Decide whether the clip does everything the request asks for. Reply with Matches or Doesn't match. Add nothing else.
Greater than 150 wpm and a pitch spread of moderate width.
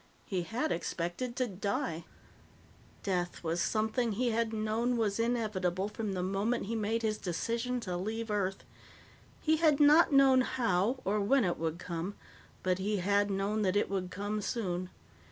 Matches